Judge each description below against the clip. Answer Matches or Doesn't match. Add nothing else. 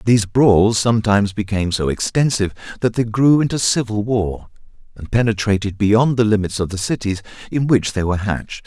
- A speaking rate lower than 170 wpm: Doesn't match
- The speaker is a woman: Doesn't match